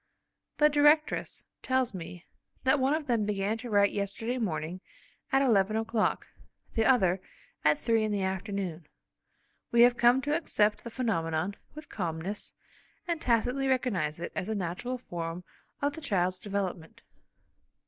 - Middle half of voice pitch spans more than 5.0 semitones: Yes, wide, 5.6 semitones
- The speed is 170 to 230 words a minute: No, average, 150 wpm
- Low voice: No, high, 215 Hz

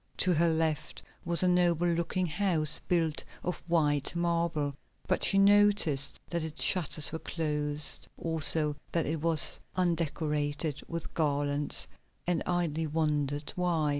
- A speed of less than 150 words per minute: Yes, slow, 135 wpm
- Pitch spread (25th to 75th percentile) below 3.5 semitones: Yes, narrow, 2.5 semitones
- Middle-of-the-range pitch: Yes, medium, 160 Hz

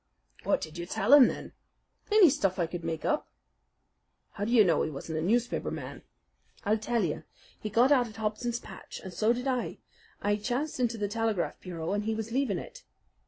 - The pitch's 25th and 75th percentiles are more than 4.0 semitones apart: Yes, average, 4.6 semitones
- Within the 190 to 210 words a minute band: Yes, fast, 205 wpm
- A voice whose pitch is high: Yes, high, 220 Hz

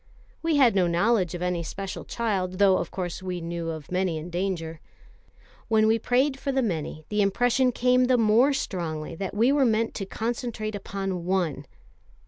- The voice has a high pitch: Yes, high, 195 Hz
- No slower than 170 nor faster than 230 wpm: Yes, average, 180 wpm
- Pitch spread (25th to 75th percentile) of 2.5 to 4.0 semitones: No, average, 5.0 semitones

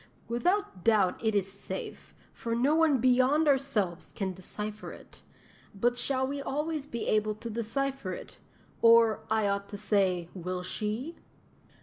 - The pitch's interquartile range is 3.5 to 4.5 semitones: No, average, 5.2 semitones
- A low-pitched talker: No, high, 230 Hz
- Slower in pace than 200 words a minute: Yes, average, 145 wpm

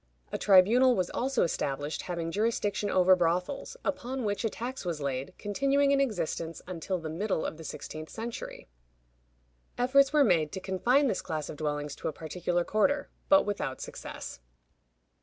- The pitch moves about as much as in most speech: No, wide, 7.3 semitones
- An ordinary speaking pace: Yes, average, 160 wpm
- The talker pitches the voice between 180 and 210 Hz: Yes, high, 190 Hz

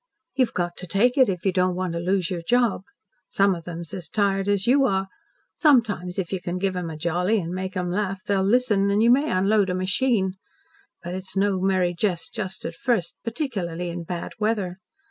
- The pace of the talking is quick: Yes, fast, 210 wpm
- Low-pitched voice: No, high, 190 Hz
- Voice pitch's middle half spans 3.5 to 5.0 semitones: No, average, 2.8 semitones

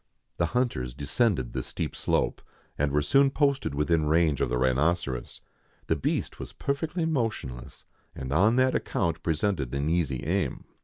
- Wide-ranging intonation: Yes, wide, 8.7 semitones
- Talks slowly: No, average, 155 wpm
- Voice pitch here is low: Yes, very low, 80 Hz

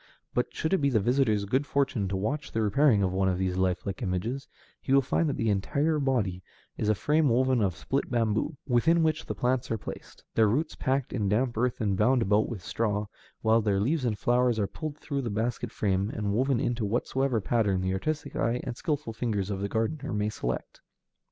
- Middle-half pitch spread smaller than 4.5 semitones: No, average, 4.8 semitones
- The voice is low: Yes, low, 115 Hz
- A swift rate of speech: Yes, fast, 215 wpm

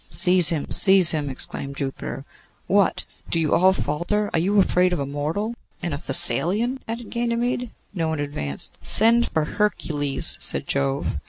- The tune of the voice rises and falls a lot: Yes, wide, 6.3 semitones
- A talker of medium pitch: Yes, medium, 175 Hz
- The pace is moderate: Yes, average, 160 wpm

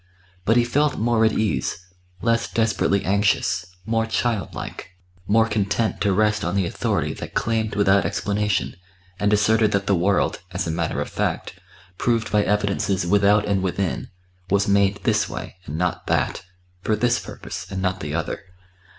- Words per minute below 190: Yes, average, 165 wpm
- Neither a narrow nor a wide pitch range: No, narrow, 2.3 semitones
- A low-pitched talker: Yes, low, 105 Hz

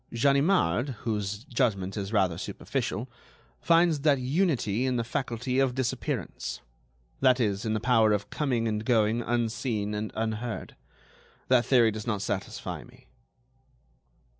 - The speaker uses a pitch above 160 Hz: No, low, 115 Hz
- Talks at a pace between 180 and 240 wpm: No, slow, 135 wpm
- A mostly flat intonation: No, average, 3.4 semitones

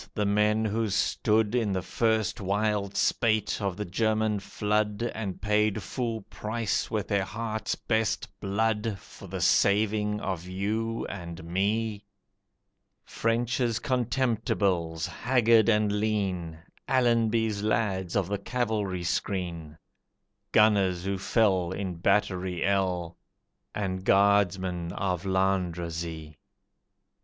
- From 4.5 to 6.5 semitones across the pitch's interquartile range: No, average, 2.8 semitones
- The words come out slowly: Yes, slow, 110 wpm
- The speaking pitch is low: Yes, low, 105 Hz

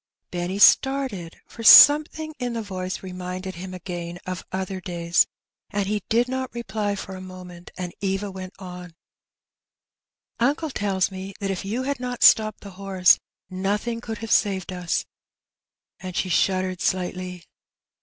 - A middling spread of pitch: Yes, average, 3.0 semitones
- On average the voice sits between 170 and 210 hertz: Yes, high, 190 Hz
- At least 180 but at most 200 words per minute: No, average, 155 wpm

